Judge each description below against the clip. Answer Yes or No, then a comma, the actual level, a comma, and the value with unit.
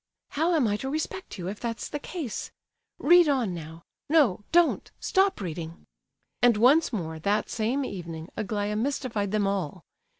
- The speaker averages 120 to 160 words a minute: Yes, average, 155 wpm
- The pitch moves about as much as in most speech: No, wide, 7.3 semitones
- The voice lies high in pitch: Yes, high, 215 Hz